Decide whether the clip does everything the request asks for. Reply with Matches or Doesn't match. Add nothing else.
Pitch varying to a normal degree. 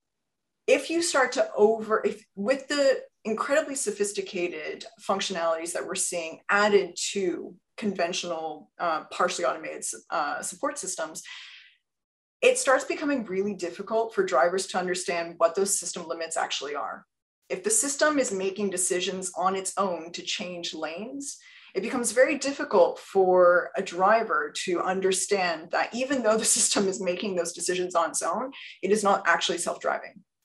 Doesn't match